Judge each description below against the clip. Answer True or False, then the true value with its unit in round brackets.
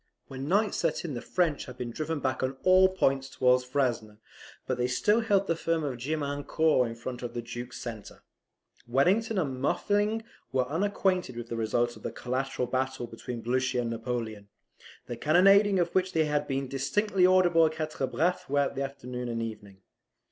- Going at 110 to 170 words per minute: False (180 wpm)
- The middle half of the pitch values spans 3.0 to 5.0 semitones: False (5.6 semitones)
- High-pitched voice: False (135 Hz)